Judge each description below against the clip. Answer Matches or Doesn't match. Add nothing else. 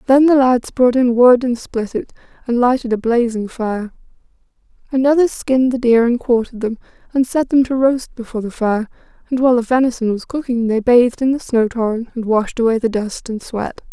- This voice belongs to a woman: Matches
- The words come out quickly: Matches